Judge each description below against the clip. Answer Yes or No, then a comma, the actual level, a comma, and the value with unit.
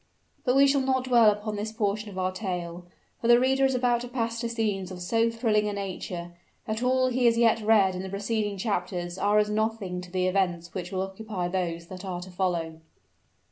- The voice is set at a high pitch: Yes, high, 205 Hz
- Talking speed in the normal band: No, fast, 215 wpm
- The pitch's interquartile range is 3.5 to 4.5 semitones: Yes, average, 3.9 semitones